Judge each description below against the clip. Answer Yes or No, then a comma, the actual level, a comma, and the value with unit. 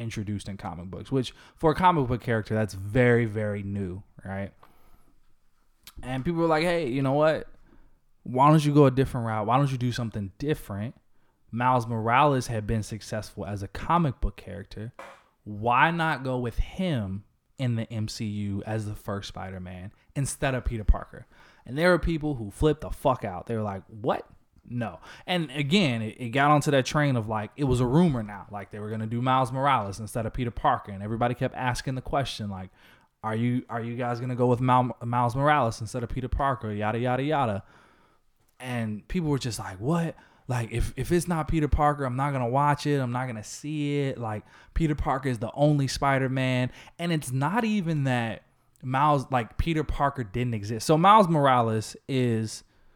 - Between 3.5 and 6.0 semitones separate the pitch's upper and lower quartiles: Yes, average, 4.7 semitones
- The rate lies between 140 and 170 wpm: No, average, 200 wpm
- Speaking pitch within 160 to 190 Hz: No, low, 125 Hz